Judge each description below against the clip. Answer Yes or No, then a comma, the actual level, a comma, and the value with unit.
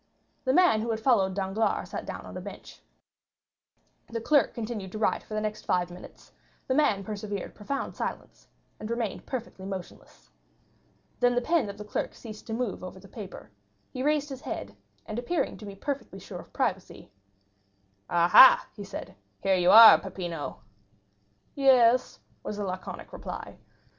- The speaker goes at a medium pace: Yes, average, 170 wpm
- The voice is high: Yes, high, 215 Hz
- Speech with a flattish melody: No, average, 4.3 semitones